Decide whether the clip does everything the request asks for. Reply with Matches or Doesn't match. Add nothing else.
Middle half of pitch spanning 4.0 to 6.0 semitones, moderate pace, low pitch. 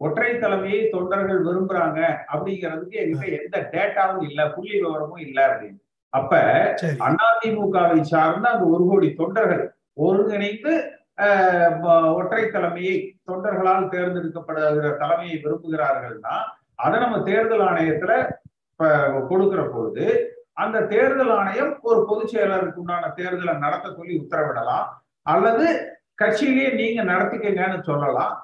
Doesn't match